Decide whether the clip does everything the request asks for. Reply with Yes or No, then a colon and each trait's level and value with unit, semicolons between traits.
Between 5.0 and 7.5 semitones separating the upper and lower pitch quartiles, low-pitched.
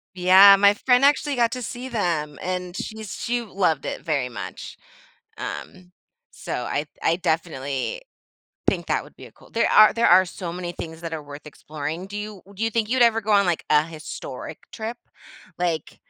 No: wide, 5.4 semitones; medium, 185 Hz